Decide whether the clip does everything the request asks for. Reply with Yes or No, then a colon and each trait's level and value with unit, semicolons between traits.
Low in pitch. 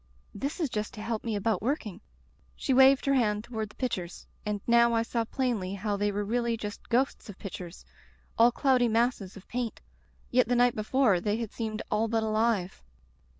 No: high, 225 Hz